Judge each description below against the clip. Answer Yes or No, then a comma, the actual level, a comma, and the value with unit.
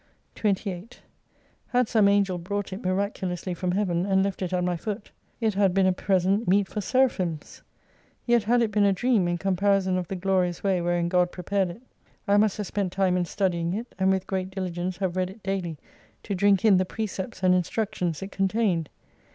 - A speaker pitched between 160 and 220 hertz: Yes, high, 190 Hz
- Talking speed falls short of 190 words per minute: No, fast, 205 wpm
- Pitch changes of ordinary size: No, narrow, 2.1 semitones